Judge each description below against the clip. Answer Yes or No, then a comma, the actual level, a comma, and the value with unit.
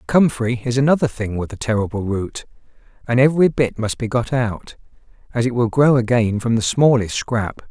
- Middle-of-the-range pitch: No, low, 120 Hz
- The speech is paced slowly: No, average, 185 wpm